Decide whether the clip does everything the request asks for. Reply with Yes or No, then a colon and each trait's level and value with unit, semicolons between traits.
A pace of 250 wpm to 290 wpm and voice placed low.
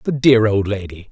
No: fast, 215 wpm; low, 110 Hz